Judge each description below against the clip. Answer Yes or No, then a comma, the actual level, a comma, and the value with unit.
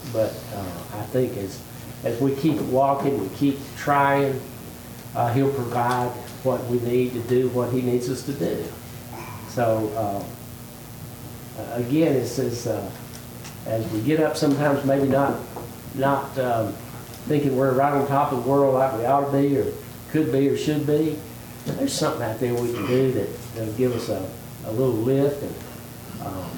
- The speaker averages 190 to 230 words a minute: No, average, 175 wpm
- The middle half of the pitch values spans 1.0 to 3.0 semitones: Yes, narrow, 2.6 semitones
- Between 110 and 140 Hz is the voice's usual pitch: Yes, low, 125 Hz